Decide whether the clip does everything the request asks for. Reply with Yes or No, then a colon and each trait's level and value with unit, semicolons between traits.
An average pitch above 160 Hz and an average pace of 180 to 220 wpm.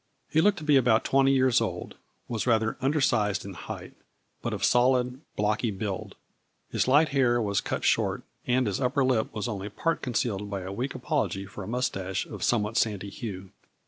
No: low, 120 Hz; average, 185 wpm